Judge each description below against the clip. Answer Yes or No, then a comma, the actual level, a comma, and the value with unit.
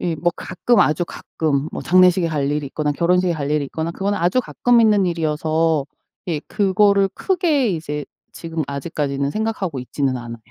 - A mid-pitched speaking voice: Yes, medium, 165 Hz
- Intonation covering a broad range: No, average, 4.6 semitones